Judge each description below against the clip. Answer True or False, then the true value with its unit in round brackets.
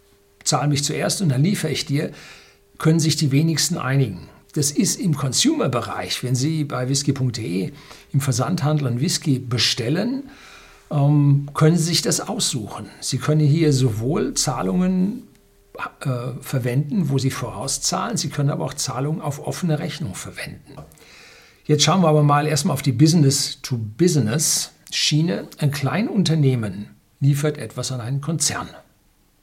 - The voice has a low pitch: False (145 Hz)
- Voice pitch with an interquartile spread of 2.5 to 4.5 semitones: True (3.2 semitones)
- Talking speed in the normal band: True (135 wpm)